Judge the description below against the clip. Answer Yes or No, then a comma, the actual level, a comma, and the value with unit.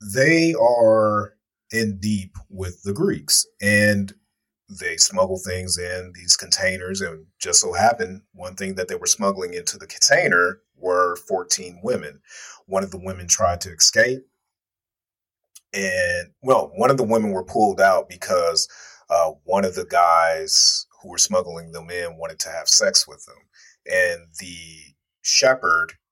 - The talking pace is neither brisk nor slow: Yes, average, 155 wpm